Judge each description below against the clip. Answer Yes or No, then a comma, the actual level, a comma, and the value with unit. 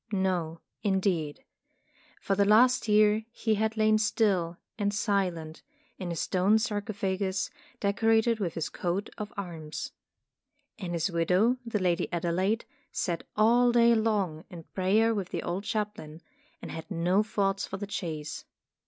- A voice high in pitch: Yes, high, 195 Hz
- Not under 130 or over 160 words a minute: Yes, average, 145 wpm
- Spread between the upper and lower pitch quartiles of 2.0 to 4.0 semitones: Yes, average, 3.7 semitones